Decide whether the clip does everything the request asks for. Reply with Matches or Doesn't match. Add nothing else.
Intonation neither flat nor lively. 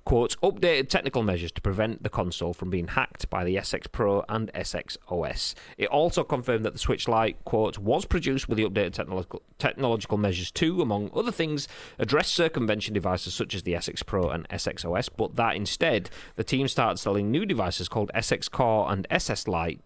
Doesn't match